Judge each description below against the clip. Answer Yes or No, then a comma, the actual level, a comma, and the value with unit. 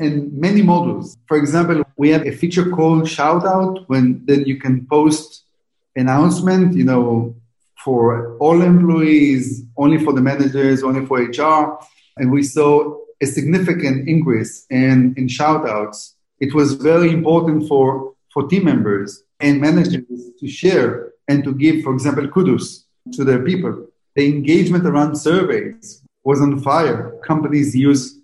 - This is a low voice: No, medium, 145 Hz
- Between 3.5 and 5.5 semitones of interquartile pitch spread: No, average, 3.1 semitones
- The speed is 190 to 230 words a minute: No, average, 145 wpm